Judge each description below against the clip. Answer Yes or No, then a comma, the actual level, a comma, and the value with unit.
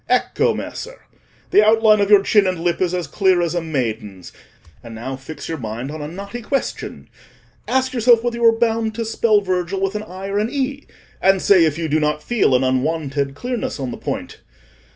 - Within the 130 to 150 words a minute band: No, fast, 205 wpm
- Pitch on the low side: No, medium, 185 Hz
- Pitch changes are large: Yes, wide, 6.8 semitones